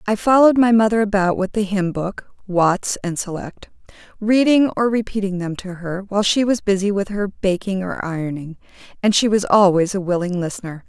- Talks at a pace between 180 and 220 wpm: Yes, average, 190 wpm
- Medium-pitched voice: No, high, 195 Hz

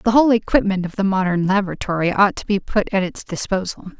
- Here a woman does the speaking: Yes, female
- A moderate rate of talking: No, fast, 210 wpm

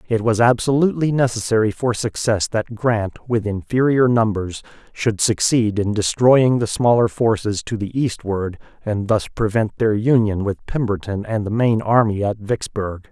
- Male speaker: Yes, male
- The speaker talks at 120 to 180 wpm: Yes, average, 155 wpm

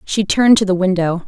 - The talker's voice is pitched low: No, high, 190 Hz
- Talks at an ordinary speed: No, fast, 235 wpm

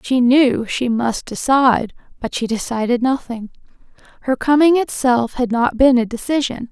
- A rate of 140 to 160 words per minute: Yes, average, 150 wpm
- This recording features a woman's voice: Yes, female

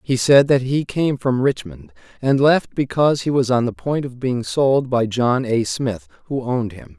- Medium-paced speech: No, fast, 215 wpm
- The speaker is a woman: No, male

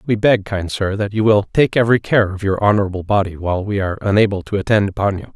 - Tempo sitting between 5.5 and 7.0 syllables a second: Yes, 6.6 syllables/s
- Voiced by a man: Yes, male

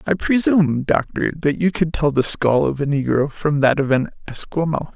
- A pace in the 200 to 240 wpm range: Yes, fast, 205 wpm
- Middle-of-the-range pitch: Yes, medium, 145 Hz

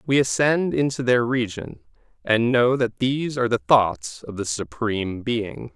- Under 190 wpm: Yes, average, 165 wpm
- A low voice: Yes, low, 120 Hz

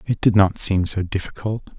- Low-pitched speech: Yes, low, 100 Hz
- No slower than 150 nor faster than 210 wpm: Yes, average, 200 wpm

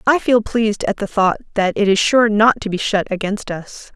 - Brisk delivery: Yes, fast, 245 wpm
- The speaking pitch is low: No, high, 210 Hz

